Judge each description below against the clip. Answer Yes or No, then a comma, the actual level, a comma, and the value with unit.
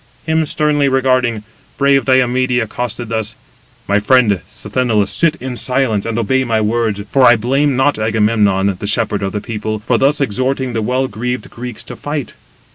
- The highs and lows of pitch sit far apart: No, average, 3.5 semitones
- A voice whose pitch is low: Yes, low, 120 Hz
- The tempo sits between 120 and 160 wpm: No, average, 175 wpm